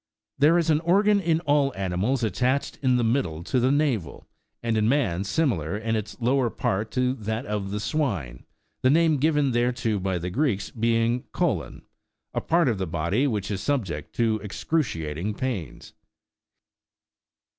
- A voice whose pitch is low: Yes, low, 115 Hz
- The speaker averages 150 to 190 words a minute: Yes, average, 165 wpm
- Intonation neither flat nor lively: No, wide, 6.0 semitones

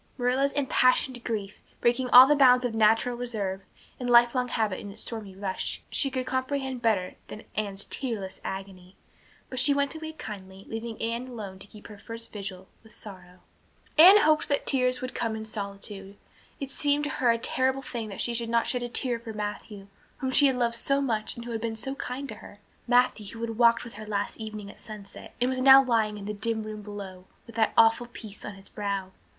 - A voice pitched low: No, high, 230 Hz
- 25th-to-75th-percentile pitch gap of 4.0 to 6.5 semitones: No, average, 3.5 semitones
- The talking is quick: Yes, fast, 215 wpm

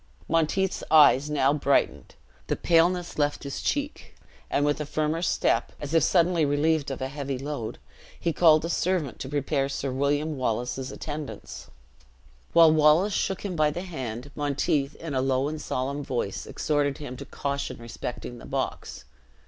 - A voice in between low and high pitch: Yes, medium, 145 Hz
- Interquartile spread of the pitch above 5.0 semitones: No, average, 2.8 semitones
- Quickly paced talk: No, average, 165 wpm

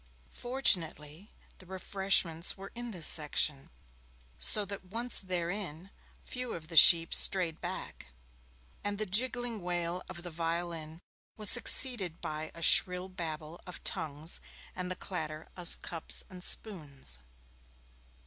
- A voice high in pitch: No, medium, 180 Hz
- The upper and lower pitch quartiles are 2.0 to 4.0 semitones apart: Yes, average, 3.5 semitones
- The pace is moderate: No, slow, 130 wpm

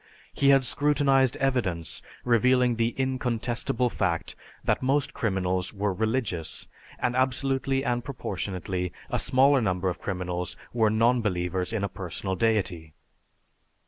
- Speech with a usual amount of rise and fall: No, wide, 5.8 semitones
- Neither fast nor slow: No, slow, 125 wpm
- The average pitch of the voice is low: Yes, low, 115 Hz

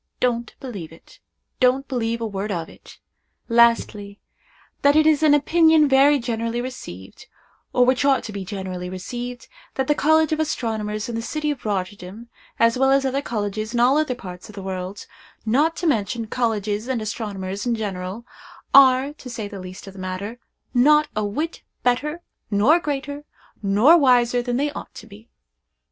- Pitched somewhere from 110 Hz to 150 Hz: No, high, 235 Hz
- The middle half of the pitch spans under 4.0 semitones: No, average, 5.0 semitones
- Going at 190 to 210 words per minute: No, average, 170 wpm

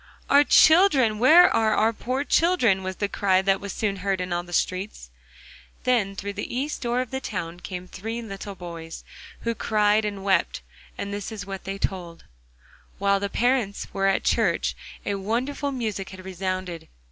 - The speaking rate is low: No, average, 180 wpm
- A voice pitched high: Yes, high, 200 Hz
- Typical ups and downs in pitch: Yes, average, 3.7 semitones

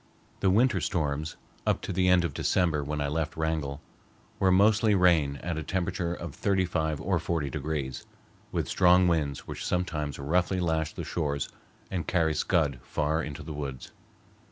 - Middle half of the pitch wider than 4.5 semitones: No, average, 3.3 semitones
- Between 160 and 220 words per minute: Yes, average, 170 wpm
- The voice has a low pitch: Yes, very low, 80 Hz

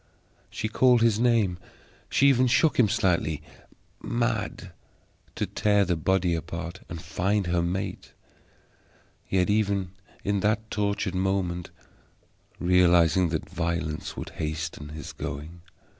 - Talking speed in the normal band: No, slow, 120 wpm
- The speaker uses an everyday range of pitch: Yes, average, 3.7 semitones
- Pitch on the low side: Yes, very low, 95 Hz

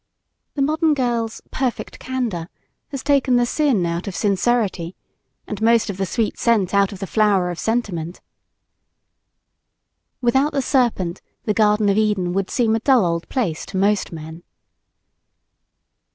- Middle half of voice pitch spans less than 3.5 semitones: No, average, 4.6 semitones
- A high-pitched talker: Yes, high, 215 Hz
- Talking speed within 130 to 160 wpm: Yes, average, 150 wpm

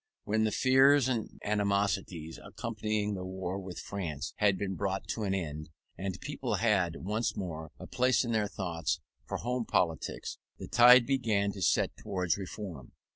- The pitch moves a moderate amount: Yes, average, 3.3 semitones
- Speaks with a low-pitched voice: Yes, low, 100 Hz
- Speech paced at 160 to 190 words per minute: Yes, average, 165 wpm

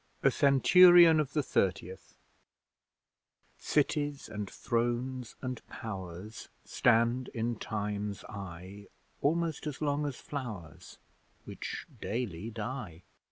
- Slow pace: Yes, slow, 100 wpm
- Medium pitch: No, low, 120 Hz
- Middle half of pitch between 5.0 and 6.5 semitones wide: Yes, wide, 5.6 semitones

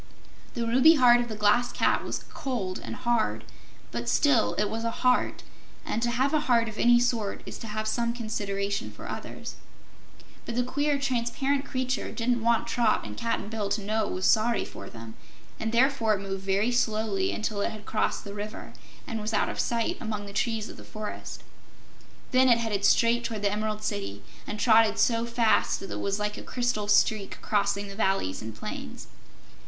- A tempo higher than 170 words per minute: Yes, average, 195 wpm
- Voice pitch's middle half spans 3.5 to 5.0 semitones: No, average, 2.7 semitones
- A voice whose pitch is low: No, high, 220 Hz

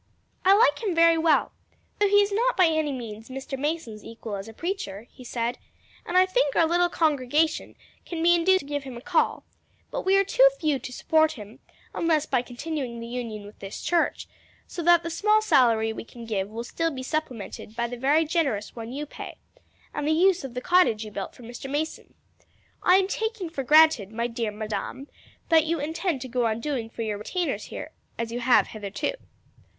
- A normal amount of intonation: No, wide, 6.4 semitones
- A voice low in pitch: No, very high, 285 Hz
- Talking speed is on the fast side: Yes, fast, 210 wpm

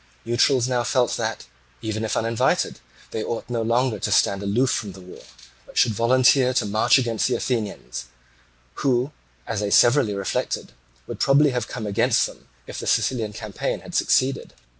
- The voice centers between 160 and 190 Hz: No, low, 115 Hz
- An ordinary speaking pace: Yes, average, 170 wpm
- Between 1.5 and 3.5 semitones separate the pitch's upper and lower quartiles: Yes, average, 3.1 semitones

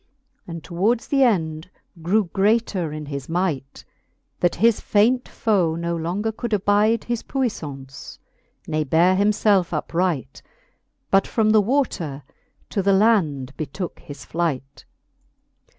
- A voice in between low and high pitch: Yes, medium, 180 Hz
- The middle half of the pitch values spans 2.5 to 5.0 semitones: No, wide, 5.5 semitones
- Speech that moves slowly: Yes, slow, 125 wpm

